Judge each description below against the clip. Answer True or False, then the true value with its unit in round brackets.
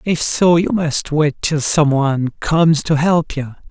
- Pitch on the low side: False (155 Hz)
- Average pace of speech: True (195 wpm)